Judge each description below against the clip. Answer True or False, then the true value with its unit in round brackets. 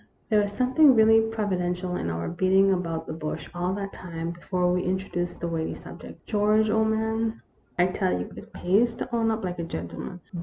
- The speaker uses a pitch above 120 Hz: True (185 Hz)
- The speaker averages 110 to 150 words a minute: False (205 wpm)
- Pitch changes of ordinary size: True (3.8 semitones)